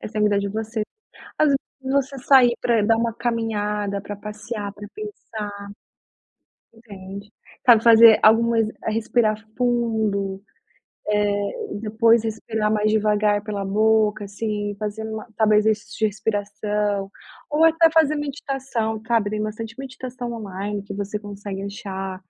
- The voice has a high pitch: Yes, high, 215 Hz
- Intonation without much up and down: Yes, narrow, 2.1 semitones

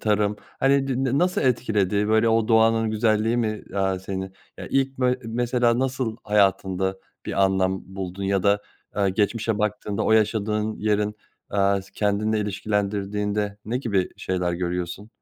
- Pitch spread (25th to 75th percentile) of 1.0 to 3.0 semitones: Yes, narrow, 2.4 semitones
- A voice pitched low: Yes, low, 105 Hz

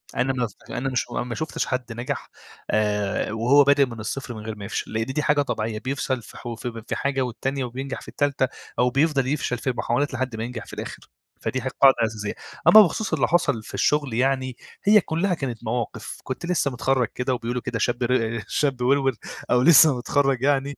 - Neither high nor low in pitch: No, low, 130 Hz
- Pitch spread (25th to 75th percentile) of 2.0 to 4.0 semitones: Yes, average, 3.0 semitones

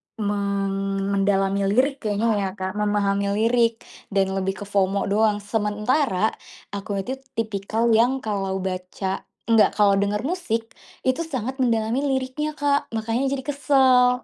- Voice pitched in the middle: No, high, 215 Hz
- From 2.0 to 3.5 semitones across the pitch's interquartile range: No, average, 4.1 semitones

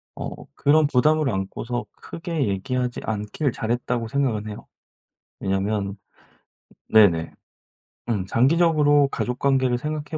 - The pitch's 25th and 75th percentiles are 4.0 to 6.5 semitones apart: Yes, wide, 5.6 semitones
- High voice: No, low, 125 Hz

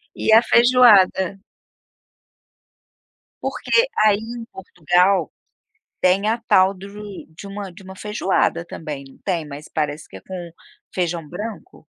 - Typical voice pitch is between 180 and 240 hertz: Yes, high, 190 Hz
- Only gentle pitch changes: No, average, 3.4 semitones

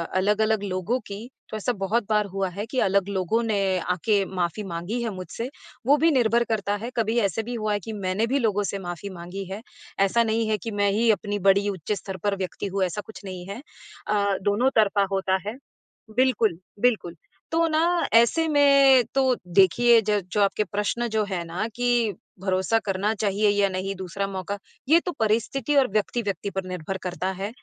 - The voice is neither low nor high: No, high, 205 Hz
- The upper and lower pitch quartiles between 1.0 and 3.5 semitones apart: Yes, average, 3.2 semitones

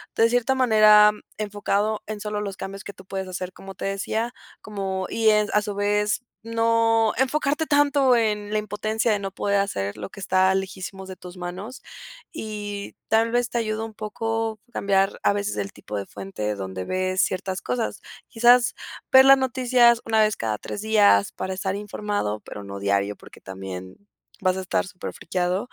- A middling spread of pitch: Yes, average, 3.2 semitones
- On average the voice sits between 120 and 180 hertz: No, high, 205 Hz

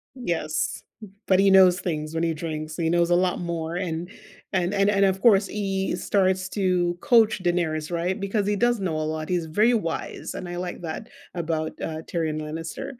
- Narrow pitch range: No, average, 3.2 semitones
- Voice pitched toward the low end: No, medium, 175 Hz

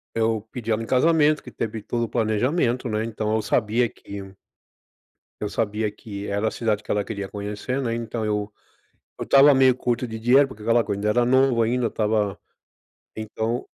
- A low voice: Yes, low, 115 Hz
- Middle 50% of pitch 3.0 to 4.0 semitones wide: No, narrow, 2.6 semitones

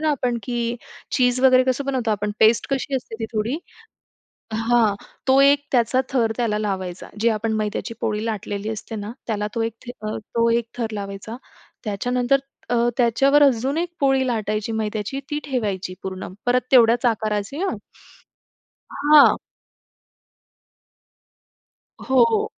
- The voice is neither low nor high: No, high, 230 Hz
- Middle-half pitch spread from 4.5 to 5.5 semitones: No, average, 3.3 semitones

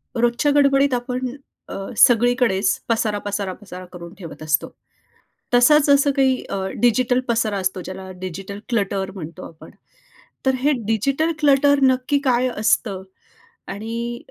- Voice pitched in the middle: No, high, 235 Hz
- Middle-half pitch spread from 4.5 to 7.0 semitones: Yes, average, 5.1 semitones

